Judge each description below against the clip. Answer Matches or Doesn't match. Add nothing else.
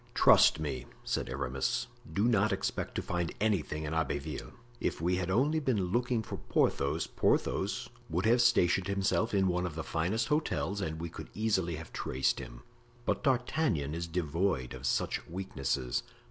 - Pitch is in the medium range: Doesn't match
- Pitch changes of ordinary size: Doesn't match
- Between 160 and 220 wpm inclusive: Matches